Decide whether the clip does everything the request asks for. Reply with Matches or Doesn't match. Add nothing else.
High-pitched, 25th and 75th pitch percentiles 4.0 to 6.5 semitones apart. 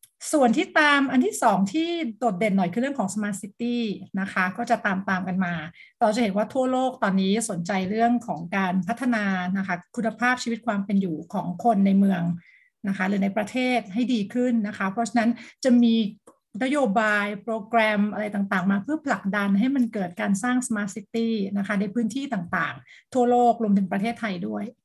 Doesn't match